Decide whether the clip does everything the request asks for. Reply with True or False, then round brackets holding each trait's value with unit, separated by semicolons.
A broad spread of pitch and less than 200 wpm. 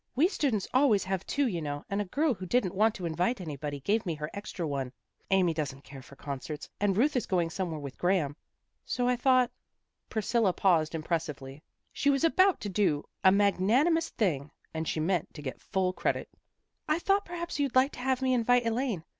False (7.9 semitones; 205 wpm)